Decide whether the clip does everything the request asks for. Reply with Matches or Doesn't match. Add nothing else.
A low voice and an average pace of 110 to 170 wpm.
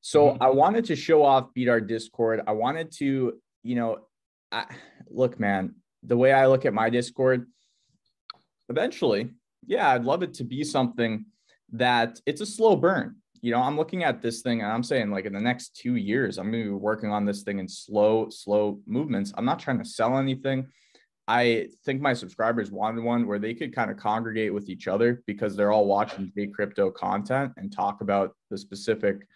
Doesn't match